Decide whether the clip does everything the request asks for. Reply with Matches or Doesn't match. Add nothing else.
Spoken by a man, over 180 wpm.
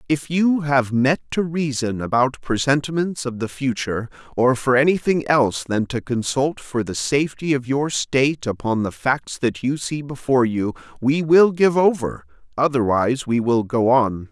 Doesn't match